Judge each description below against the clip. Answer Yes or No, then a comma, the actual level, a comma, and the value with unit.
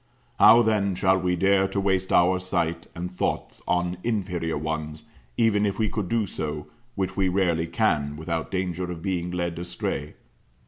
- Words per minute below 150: No, average, 170 wpm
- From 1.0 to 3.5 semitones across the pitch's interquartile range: Yes, average, 2.7 semitones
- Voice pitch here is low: Yes, very low, 90 Hz